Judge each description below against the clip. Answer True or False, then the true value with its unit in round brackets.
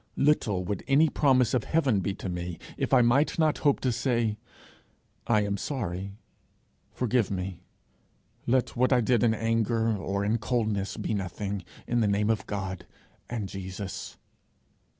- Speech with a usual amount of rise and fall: True (4.0 semitones)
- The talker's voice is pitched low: True (110 Hz)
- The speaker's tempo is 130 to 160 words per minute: True (155 wpm)